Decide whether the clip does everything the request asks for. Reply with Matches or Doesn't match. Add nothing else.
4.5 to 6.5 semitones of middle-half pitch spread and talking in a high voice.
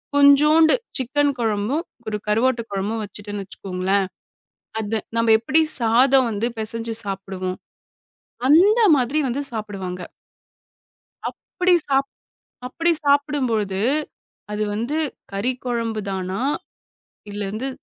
Matches